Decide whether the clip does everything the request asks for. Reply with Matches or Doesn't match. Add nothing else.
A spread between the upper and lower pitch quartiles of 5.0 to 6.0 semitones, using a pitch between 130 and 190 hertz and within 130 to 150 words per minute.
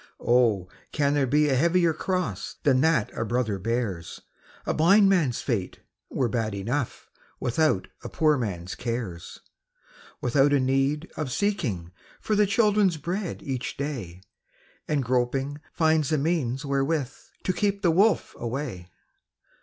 Matches